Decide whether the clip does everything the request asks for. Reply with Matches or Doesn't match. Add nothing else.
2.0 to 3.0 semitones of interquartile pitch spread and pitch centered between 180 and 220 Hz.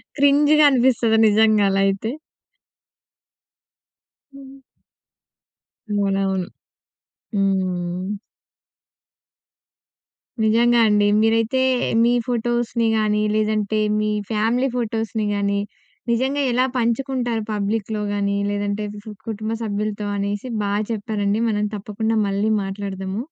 Matches